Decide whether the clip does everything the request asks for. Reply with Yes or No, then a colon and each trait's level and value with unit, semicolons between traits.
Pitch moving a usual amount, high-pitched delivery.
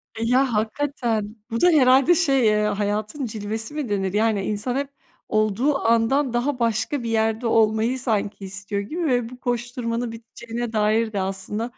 Yes: average, 3.0 semitones; high, 230 Hz